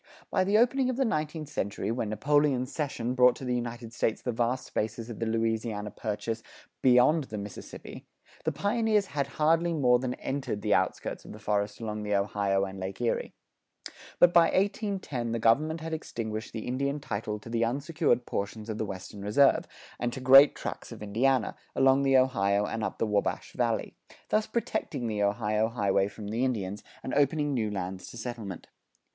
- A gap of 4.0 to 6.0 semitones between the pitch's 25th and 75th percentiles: Yes, average, 5.1 semitones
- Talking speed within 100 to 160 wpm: No, average, 185 wpm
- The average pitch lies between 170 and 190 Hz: No, low, 120 Hz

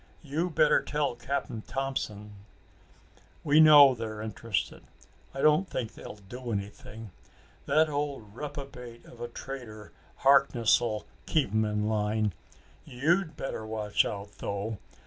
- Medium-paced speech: No, slow, 125 wpm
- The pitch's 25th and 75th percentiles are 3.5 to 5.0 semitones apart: Yes, average, 4.7 semitones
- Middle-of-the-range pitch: No, low, 120 Hz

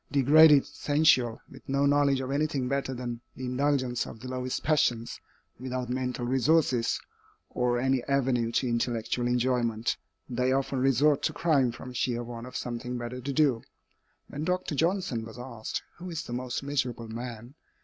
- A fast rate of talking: No, average, 160 wpm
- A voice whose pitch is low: Yes, low, 130 Hz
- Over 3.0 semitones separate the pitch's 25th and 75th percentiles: No, narrow, 2.5 semitones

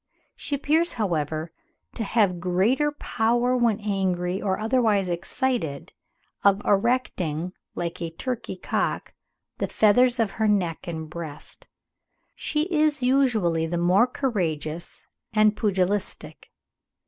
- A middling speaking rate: No, slow, 115 wpm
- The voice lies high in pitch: Yes, high, 205 Hz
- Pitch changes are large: Yes, wide, 6.0 semitones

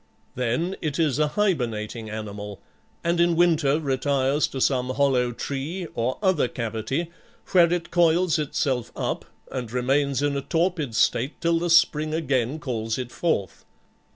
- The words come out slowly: No, average, 150 wpm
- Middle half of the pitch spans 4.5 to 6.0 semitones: Yes, average, 5.1 semitones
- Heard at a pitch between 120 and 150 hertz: Yes, medium, 140 Hz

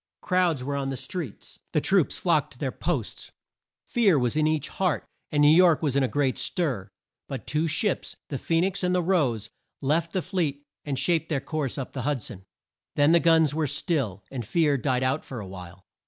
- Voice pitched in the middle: Yes, medium, 145 Hz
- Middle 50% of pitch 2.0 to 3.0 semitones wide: No, average, 4.1 semitones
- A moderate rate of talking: No, fast, 210 wpm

